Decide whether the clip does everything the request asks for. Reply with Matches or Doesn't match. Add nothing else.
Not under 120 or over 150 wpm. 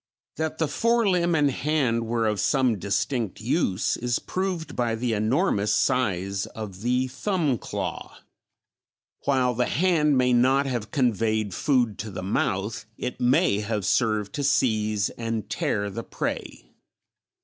Matches